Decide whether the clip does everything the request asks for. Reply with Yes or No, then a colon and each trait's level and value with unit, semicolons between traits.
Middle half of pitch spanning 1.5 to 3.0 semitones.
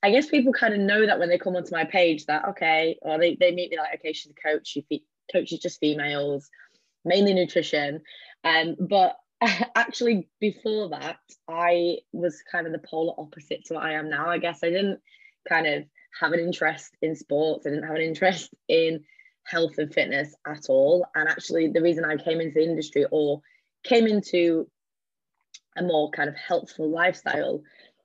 No: average, 3.7 semitones